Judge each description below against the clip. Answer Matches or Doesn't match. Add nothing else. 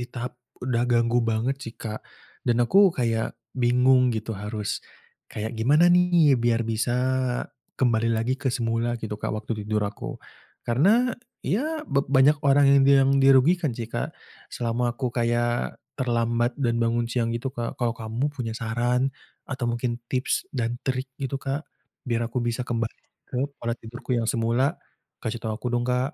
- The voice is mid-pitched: Doesn't match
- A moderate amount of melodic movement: Doesn't match